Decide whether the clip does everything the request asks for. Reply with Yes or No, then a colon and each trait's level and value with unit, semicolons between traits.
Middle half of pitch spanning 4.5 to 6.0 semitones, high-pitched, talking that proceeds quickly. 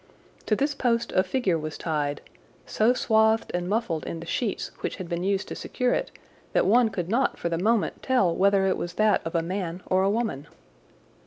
Yes: average, 4.8 semitones; high, 195 Hz; fast, 210 wpm